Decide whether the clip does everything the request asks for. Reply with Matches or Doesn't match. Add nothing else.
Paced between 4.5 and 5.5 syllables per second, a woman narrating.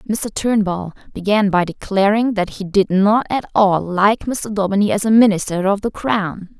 Matches